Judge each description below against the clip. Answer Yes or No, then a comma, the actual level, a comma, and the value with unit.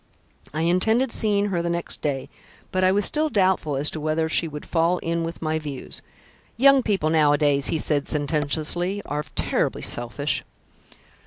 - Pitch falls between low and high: Yes, medium, 165 Hz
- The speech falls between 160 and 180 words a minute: Yes, average, 165 wpm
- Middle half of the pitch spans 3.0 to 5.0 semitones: Yes, average, 3.9 semitones